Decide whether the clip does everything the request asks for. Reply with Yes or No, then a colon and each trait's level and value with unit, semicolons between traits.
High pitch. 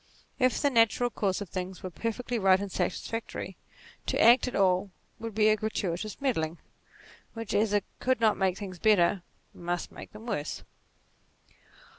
Yes: high, 205 Hz